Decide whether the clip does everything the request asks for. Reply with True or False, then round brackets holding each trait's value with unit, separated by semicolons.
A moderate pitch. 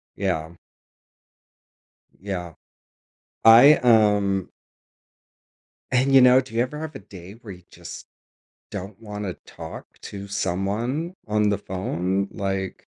False (100 Hz)